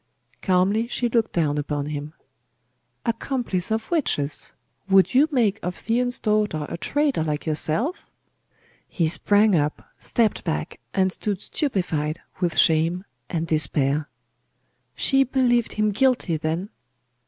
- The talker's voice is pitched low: No, high, 190 Hz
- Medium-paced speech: No, slow, 125 wpm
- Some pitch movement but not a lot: No, wide, 6.9 semitones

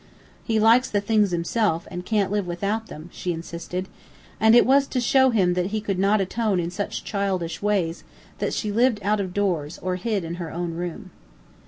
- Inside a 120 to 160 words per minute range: No, average, 200 wpm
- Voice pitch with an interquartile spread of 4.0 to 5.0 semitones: No, average, 3.6 semitones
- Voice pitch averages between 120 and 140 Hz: No, high, 195 Hz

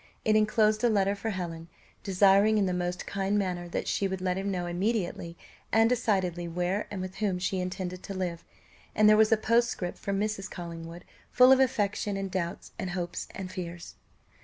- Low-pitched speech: No, high, 190 Hz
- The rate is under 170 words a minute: No, average, 190 wpm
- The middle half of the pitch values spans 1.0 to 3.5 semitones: Yes, average, 3.0 semitones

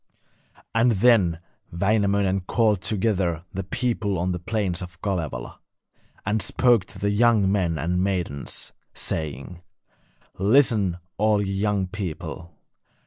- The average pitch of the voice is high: No, very low, 95 Hz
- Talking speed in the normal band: No, slow, 120 wpm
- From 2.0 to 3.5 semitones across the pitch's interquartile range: Yes, average, 3.2 semitones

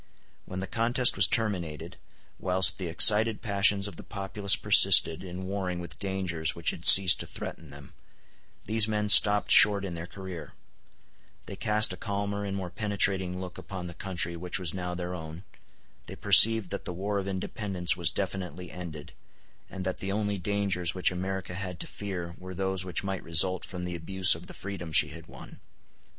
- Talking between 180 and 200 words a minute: Yes, average, 185 wpm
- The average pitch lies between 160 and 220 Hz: No, very low, 95 Hz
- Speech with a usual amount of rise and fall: No, narrow, 2.2 semitones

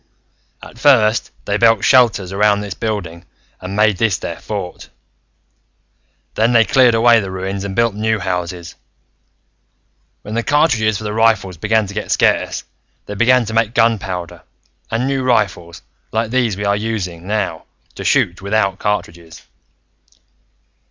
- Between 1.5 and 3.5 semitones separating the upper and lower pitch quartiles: Yes, average, 2.9 semitones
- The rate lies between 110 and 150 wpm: Yes, average, 145 wpm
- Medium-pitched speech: No, low, 105 Hz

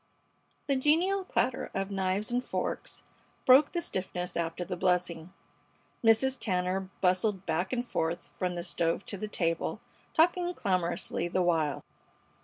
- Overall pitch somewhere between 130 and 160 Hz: No, high, 190 Hz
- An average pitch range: No, wide, 5.9 semitones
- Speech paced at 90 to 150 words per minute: Yes, average, 140 wpm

